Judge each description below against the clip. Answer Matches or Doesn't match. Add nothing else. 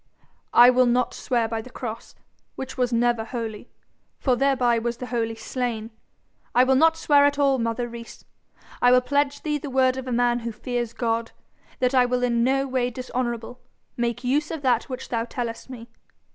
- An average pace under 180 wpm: Doesn't match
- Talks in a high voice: Matches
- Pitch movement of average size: Doesn't match